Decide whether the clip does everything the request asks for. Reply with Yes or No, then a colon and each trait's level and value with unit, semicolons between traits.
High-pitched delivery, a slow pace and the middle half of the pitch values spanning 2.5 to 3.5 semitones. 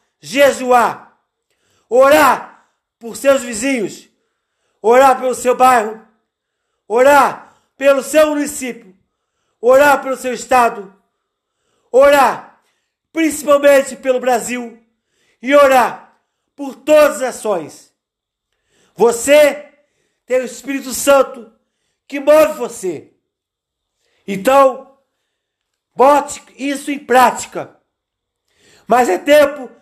Yes: very high, 275 Hz; slow, 85 wpm; average, 3.1 semitones